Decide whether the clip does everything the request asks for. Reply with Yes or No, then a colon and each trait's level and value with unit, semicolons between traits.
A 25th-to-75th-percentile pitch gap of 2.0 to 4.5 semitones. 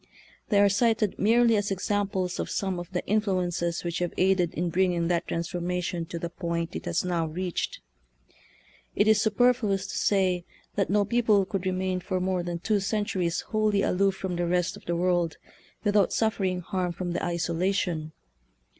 Yes: average, 2.7 semitones